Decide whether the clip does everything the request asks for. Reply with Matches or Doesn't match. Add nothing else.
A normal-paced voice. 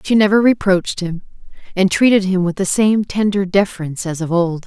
Matches